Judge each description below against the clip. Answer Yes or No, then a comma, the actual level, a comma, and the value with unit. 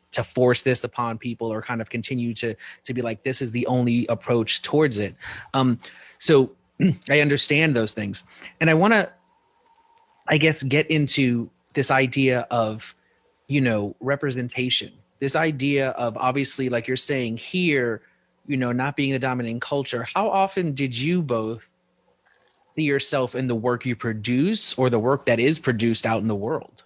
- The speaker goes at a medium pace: Yes, average, 170 wpm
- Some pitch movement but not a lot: Yes, average, 3.4 semitones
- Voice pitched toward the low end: Yes, low, 130 Hz